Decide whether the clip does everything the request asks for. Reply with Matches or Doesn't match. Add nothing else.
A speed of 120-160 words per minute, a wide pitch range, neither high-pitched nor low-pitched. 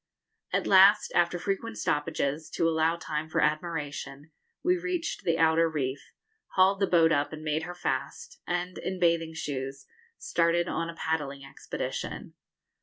Doesn't match